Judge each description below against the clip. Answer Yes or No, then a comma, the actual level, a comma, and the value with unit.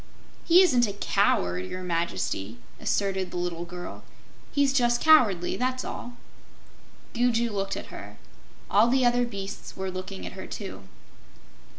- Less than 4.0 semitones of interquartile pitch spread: No, average, 5.3 semitones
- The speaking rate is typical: Yes, average, 145 wpm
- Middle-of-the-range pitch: No, high, 200 Hz